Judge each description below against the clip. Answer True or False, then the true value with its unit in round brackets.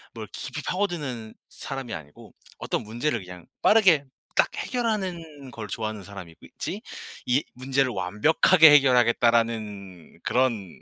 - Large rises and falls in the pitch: True (5.9 semitones)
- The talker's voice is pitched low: True (120 Hz)